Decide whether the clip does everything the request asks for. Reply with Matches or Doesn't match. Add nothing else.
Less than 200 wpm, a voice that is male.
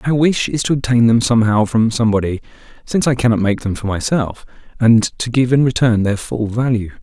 Doesn't match